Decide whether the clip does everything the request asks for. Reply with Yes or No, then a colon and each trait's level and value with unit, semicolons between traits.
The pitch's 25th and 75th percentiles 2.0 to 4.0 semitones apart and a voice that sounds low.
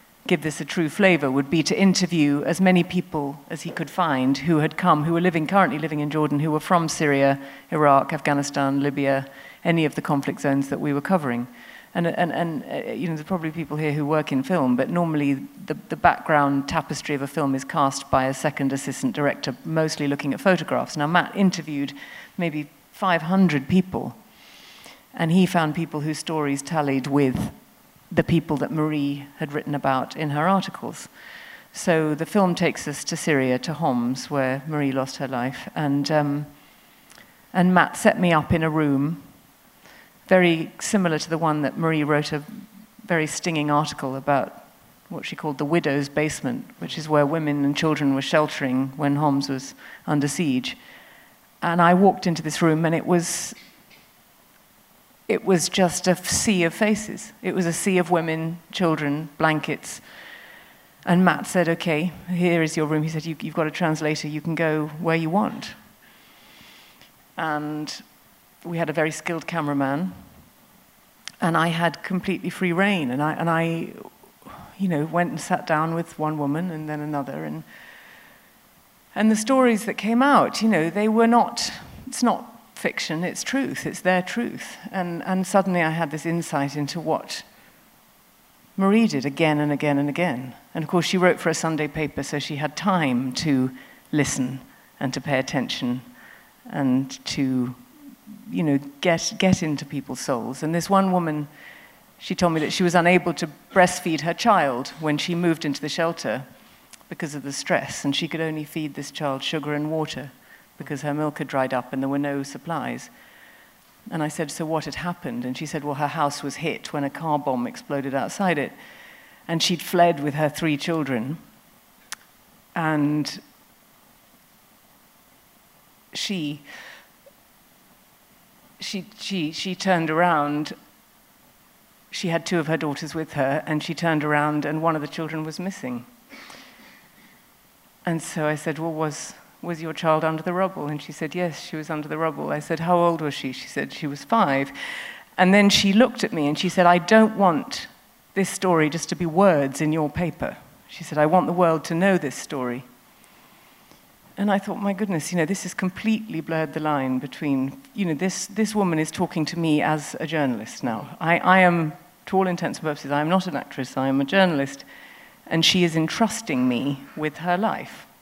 No: average, 3.7 semitones; medium, 160 Hz